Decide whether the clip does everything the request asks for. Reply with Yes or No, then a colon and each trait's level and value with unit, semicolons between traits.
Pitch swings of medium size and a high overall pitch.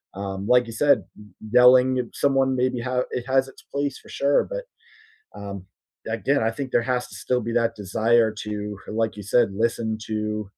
No: average, 3.2 semitones; low, 120 Hz